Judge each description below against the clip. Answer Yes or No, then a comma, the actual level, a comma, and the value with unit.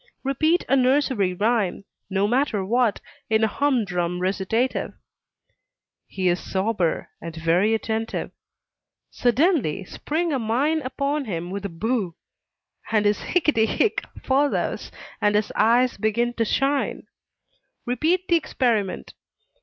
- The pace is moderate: No, slow, 120 wpm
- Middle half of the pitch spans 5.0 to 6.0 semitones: Yes, wide, 5.4 semitones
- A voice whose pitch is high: Yes, high, 225 Hz